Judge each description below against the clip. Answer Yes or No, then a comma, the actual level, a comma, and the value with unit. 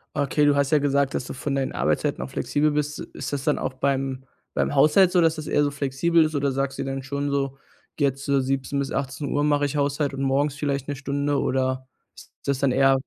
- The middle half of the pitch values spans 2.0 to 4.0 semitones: No, narrow, 1.2 semitones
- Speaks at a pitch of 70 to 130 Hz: No, medium, 140 Hz